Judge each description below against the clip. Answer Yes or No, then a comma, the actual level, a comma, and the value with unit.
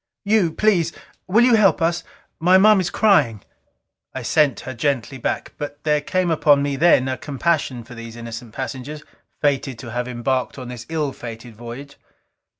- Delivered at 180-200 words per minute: No, average, 170 wpm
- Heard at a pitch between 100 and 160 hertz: Yes, medium, 140 Hz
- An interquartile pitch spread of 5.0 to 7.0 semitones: Yes, average, 5.3 semitones